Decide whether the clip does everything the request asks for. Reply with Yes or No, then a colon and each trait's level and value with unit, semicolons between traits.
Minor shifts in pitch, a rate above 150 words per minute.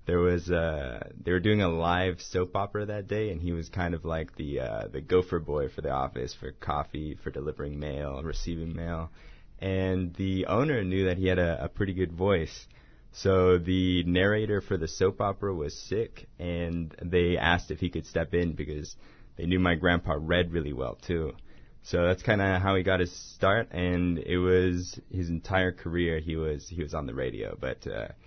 Yes: narrow, 2.3 semitones; fast, 205 wpm